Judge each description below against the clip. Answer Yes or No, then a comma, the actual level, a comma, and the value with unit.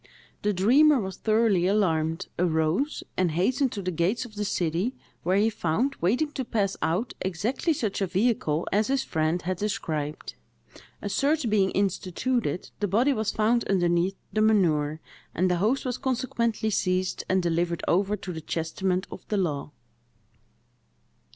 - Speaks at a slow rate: No, average, 155 wpm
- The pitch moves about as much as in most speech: Yes, average, 4.7 semitones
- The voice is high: Yes, high, 195 Hz